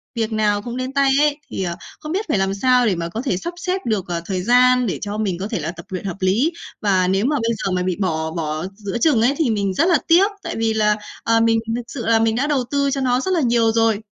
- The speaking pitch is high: Yes, high, 225 Hz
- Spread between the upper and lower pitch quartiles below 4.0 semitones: No, average, 5.0 semitones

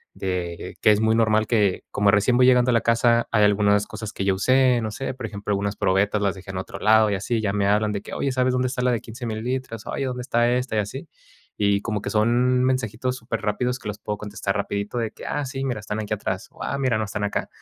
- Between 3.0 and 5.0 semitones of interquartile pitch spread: Yes, average, 3.3 semitones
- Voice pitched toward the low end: Yes, low, 110 Hz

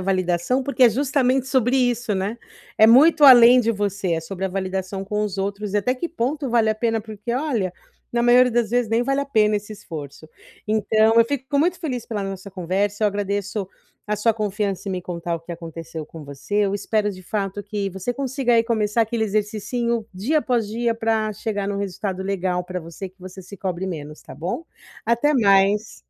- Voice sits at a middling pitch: No, high, 210 Hz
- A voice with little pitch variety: No, average, 3.8 semitones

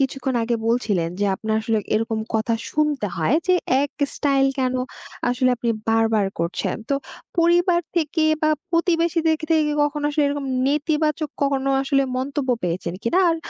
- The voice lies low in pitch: No, very high, 275 Hz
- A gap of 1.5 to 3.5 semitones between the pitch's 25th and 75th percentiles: No, average, 5.1 semitones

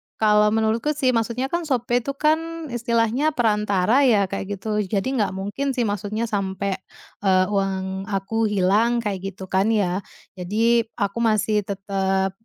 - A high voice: Yes, high, 210 Hz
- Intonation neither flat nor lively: Yes, average, 3.4 semitones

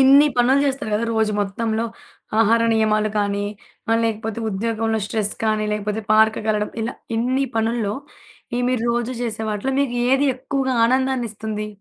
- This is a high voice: Yes, high, 225 Hz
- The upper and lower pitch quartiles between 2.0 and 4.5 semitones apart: Yes, average, 2.7 semitones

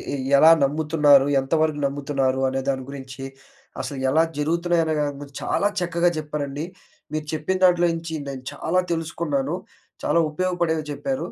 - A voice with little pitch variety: No, average, 3.1 semitones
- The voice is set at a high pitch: No, medium, 155 Hz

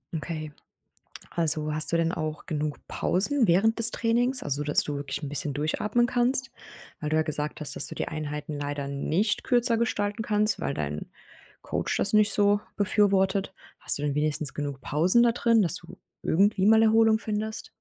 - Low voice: No, medium, 180 Hz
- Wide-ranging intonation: Yes, wide, 6.6 semitones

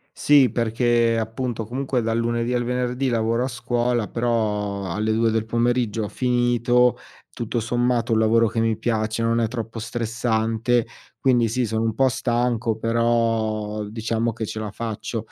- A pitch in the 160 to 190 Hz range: No, low, 115 Hz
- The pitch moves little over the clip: Yes, narrow, 1.5 semitones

